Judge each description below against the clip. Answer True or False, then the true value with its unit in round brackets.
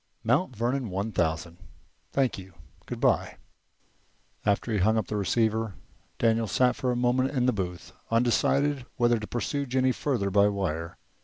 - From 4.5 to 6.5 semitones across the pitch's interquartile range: False (4.1 semitones)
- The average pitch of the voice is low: True (115 Hz)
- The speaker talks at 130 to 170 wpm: True (160 wpm)